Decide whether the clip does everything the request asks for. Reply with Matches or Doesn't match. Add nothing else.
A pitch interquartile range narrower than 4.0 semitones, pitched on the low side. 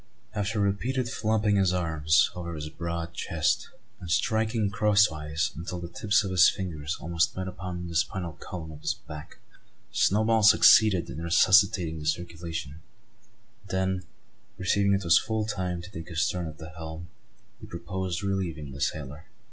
Matches